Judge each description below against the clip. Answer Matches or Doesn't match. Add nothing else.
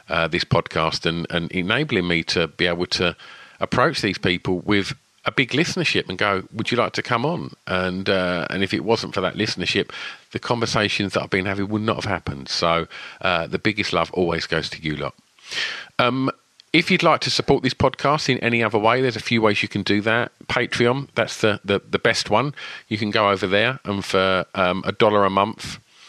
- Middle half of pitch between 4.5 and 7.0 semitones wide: Matches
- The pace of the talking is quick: Matches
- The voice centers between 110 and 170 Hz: Doesn't match